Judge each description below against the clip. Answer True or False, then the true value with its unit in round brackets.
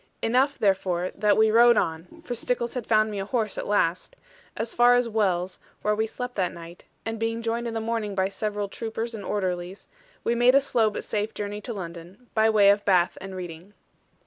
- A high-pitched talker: True (215 Hz)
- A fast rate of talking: True (210 wpm)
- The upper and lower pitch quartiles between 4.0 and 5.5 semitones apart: False (3.3 semitones)